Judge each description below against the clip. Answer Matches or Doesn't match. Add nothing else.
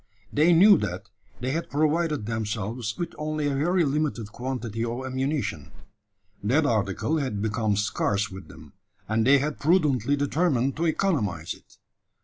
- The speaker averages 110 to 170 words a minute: Matches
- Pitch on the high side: Doesn't match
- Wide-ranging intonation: Matches